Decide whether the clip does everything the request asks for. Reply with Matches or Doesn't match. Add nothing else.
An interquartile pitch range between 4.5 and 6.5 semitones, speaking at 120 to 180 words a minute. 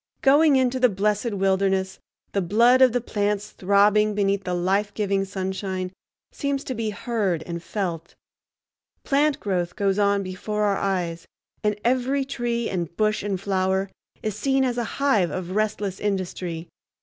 Doesn't match